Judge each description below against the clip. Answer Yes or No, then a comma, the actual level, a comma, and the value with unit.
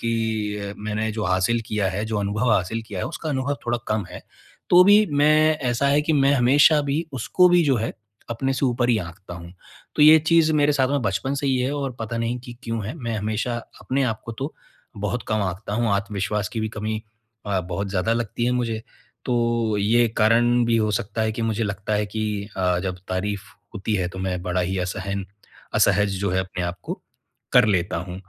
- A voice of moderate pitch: No, low, 110 Hz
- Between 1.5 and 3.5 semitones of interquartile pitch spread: No, average, 3.9 semitones